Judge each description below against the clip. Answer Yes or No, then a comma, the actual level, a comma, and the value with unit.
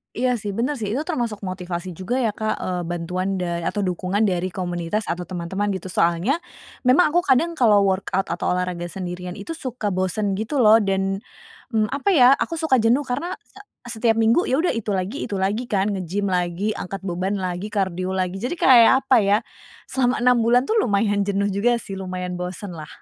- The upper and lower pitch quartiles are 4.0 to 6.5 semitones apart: Yes, average, 4.4 semitones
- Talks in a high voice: Yes, high, 200 Hz